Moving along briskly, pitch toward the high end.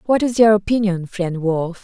No: average, 195 wpm; high, 195 Hz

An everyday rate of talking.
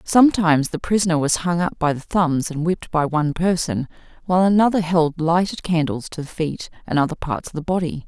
No: fast, 210 wpm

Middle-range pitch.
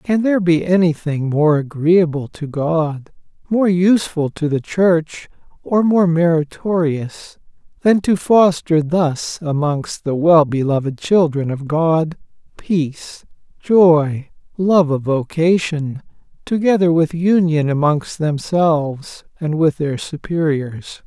Yes: medium, 160 Hz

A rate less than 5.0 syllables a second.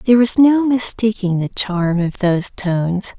Yes: 4.6 syllables/s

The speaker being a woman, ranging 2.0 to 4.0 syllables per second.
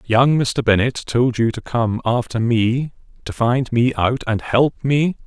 No: male; 3.9 syllables/s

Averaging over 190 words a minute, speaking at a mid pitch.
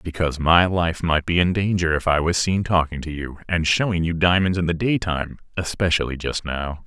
No: average, 200 wpm; very low, 85 Hz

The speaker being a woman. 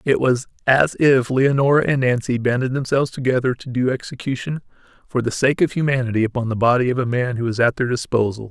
No: male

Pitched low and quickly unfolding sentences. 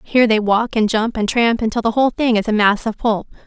No: high, 225 Hz; fast, 275 wpm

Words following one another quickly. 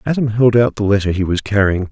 Yes: fast, 250 wpm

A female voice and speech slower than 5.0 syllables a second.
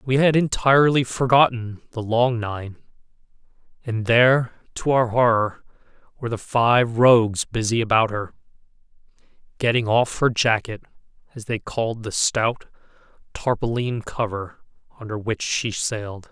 No: male; 4.6 syllables/s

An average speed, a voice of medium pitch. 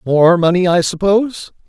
Yes: average, 145 wpm; medium, 180 Hz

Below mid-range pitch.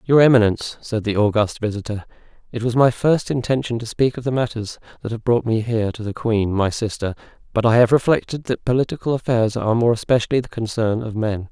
Yes: low, 115 Hz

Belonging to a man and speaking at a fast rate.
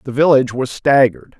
No: male; average, 175 wpm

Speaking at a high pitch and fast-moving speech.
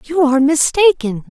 No: very high, 295 Hz; slow, 135 wpm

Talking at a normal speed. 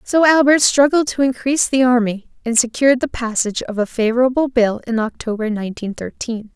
Yes: average, 175 wpm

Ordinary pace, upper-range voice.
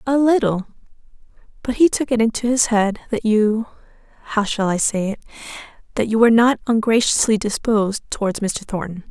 Yes: average, 150 wpm; high, 220 Hz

